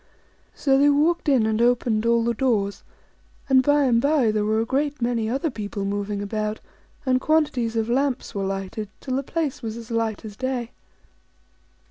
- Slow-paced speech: No, average, 180 wpm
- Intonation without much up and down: No, average, 3.8 semitones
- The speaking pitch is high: Yes, high, 235 Hz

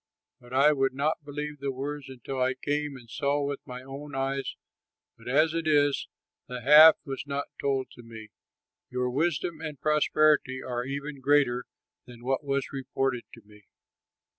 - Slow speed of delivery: No, average, 165 wpm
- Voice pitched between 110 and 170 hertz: Yes, medium, 140 Hz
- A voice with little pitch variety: Yes, narrow, 2.3 semitones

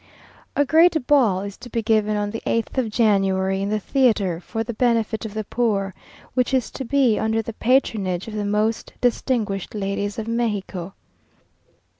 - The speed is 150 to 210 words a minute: Yes, average, 175 wpm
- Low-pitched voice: No, high, 220 Hz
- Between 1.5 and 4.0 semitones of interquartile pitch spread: Yes, average, 3.1 semitones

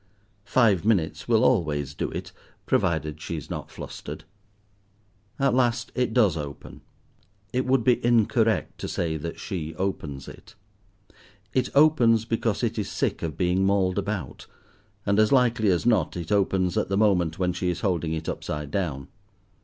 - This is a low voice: Yes, very low, 95 Hz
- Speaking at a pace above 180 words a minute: No, average, 160 wpm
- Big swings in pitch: Yes, wide, 5.7 semitones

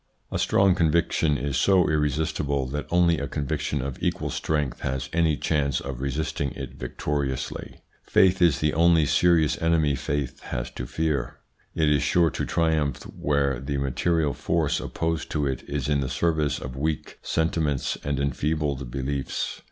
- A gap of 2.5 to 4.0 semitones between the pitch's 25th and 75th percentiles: Yes, average, 2.8 semitones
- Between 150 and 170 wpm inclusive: Yes, average, 160 wpm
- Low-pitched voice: Yes, very low, 75 Hz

